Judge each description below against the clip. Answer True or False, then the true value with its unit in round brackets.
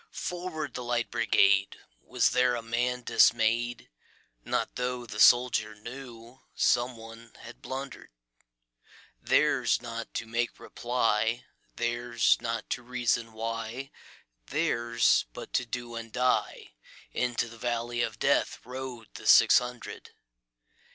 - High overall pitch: False (120 Hz)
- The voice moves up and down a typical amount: False (1.5 semitones)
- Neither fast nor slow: False (100 wpm)